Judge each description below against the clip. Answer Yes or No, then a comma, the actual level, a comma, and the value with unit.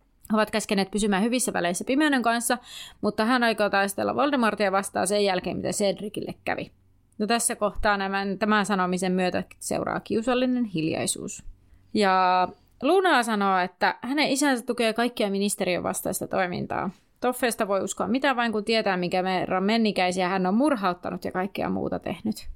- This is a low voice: No, high, 205 Hz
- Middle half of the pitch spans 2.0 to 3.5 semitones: No, average, 4.1 semitones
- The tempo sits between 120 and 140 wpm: No, average, 150 wpm